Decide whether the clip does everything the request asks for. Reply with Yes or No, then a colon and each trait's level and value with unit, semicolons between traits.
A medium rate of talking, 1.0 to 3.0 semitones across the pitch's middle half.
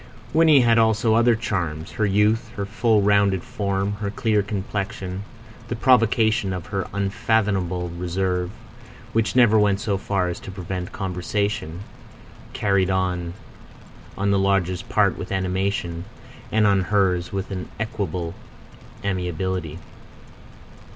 No: slow, 125 wpm; narrow, 2.6 semitones